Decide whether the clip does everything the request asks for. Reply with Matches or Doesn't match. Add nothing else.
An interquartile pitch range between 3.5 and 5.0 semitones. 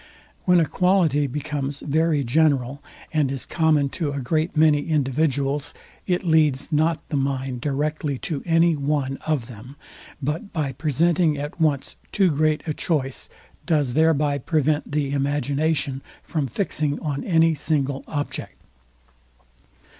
Doesn't match